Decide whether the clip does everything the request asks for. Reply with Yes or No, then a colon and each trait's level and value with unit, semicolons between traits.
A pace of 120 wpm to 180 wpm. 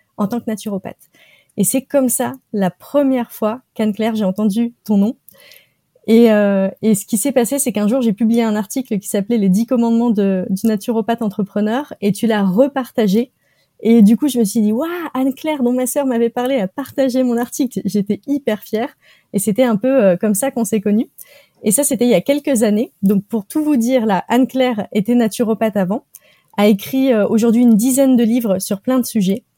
No: average, 215 wpm